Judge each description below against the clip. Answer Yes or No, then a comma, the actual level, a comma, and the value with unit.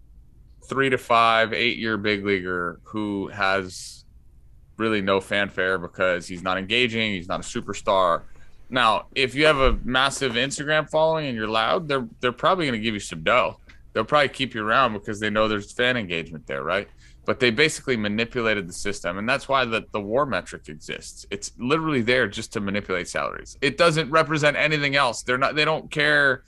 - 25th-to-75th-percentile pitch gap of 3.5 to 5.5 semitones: Yes, average, 5.2 semitones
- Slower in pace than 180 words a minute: No, average, 190 wpm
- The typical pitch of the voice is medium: No, low, 115 Hz